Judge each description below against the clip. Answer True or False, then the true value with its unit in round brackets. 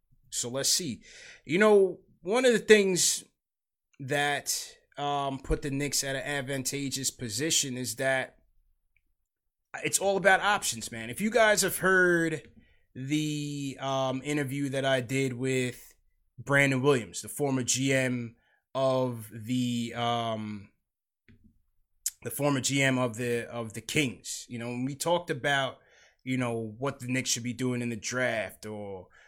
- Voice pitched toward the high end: False (130 Hz)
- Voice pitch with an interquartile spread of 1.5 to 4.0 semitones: True (3.3 semitones)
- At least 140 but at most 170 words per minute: True (145 wpm)